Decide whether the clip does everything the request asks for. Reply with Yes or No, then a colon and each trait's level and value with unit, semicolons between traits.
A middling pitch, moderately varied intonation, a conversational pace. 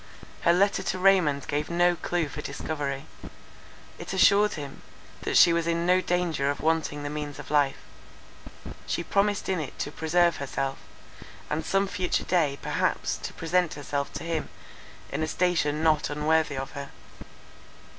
Yes: medium, 160 Hz; average, 3.4 semitones; average, 160 wpm